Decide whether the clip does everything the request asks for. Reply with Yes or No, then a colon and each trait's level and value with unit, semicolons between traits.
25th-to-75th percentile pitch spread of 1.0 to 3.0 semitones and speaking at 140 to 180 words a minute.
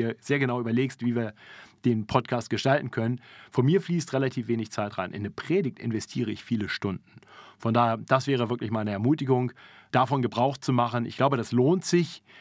No: narrow, 2.6 semitones; fast, 190 wpm